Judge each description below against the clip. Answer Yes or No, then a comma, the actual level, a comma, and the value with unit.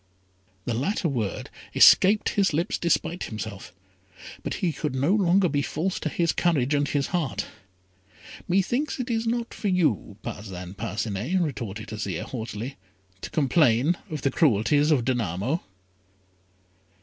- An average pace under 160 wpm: Yes, slow, 135 wpm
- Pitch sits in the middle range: Yes, medium, 145 Hz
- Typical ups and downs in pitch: No, wide, 7.9 semitones